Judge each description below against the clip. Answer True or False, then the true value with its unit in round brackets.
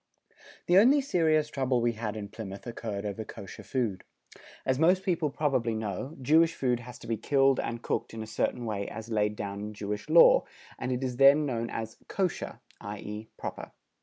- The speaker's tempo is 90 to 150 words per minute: False (190 wpm)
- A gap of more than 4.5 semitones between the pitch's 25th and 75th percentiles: True (5.3 semitones)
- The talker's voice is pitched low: True (120 Hz)